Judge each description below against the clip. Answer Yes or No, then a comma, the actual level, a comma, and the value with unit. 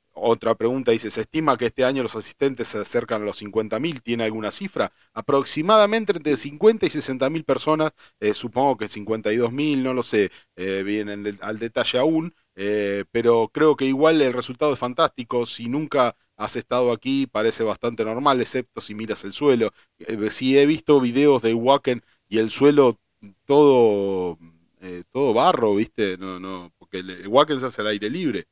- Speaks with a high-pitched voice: No, low, 120 Hz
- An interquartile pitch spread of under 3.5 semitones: No, average, 5.0 semitones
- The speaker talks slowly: No, average, 175 wpm